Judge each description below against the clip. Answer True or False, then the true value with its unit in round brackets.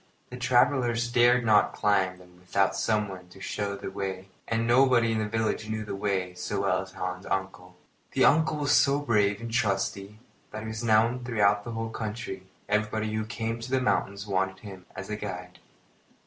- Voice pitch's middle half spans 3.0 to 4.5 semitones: True (3.3 semitones)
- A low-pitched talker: True (105 Hz)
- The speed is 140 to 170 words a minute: False (190 wpm)